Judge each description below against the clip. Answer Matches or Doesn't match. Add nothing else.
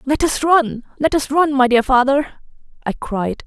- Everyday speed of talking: Matches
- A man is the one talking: Doesn't match